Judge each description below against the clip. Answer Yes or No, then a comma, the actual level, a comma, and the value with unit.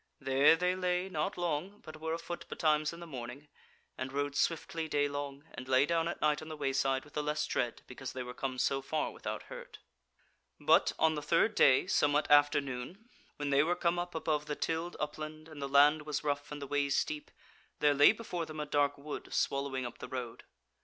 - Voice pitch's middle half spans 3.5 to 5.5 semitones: No, narrow, 2.6 semitones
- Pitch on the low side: No, medium, 150 Hz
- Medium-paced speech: No, fast, 210 wpm